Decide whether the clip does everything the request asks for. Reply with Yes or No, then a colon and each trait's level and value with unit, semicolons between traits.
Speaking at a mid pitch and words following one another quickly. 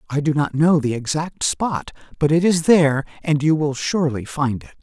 Yes: medium, 150 Hz; fast, 210 wpm